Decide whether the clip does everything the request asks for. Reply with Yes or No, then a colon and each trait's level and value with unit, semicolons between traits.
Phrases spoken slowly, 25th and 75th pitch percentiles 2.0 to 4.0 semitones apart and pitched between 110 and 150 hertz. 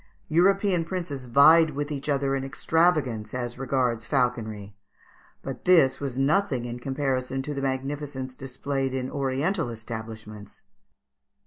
Yes: slow, 125 wpm; average, 2.9 semitones; low, 135 Hz